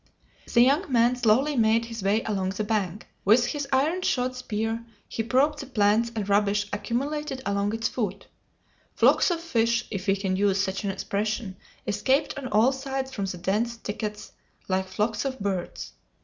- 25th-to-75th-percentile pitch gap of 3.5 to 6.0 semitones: Yes, average, 4.0 semitones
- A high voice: Yes, high, 225 Hz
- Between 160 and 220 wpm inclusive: Yes, average, 175 wpm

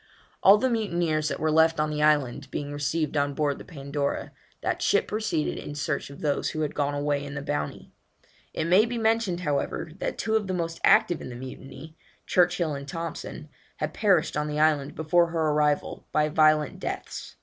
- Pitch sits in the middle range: Yes, medium, 155 Hz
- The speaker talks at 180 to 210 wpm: Yes, average, 195 wpm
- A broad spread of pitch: No, average, 3.0 semitones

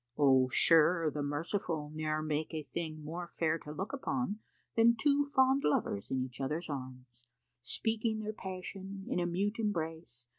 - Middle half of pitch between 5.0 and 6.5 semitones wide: Yes, wide, 5.6 semitones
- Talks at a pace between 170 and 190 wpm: No, average, 160 wpm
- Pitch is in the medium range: Yes, medium, 165 Hz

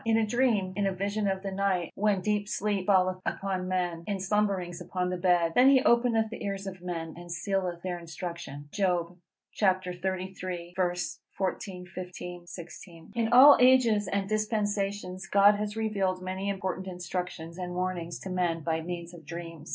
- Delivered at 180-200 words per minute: No, average, 165 wpm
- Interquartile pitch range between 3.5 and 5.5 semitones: No, narrow, 2.5 semitones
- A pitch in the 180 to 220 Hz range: Yes, medium, 185 Hz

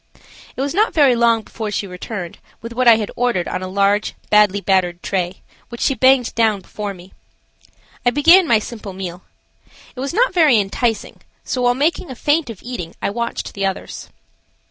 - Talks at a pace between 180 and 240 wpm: Yes, average, 190 wpm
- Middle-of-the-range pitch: No, high, 225 Hz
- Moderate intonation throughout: Yes, average, 4.5 semitones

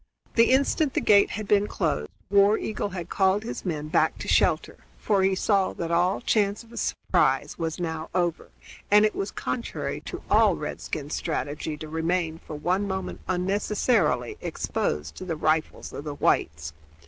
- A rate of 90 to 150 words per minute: No, average, 170 wpm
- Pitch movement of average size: Yes, average, 4.5 semitones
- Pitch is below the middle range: No, medium, 180 Hz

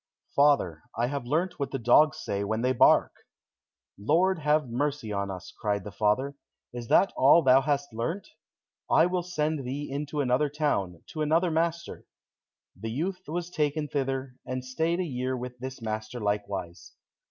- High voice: No, low, 135 Hz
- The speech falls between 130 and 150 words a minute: No, average, 165 wpm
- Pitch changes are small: No, average, 4.8 semitones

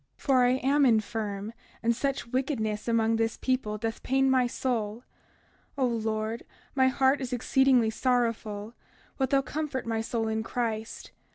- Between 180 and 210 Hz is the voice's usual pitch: No, high, 235 Hz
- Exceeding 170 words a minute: No, average, 155 wpm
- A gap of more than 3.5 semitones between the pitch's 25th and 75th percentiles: No, average, 2.9 semitones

